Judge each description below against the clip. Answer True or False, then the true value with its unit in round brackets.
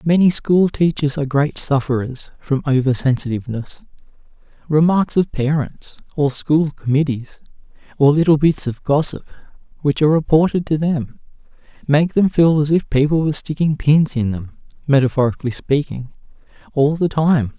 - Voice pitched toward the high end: False (145 Hz)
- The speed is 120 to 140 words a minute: True (135 wpm)